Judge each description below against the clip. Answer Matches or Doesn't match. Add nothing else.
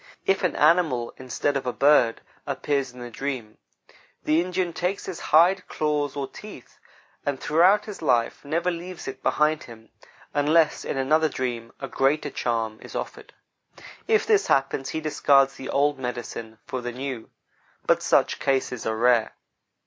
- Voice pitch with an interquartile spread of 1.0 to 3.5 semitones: Doesn't match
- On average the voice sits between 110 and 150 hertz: Matches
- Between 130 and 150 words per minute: Doesn't match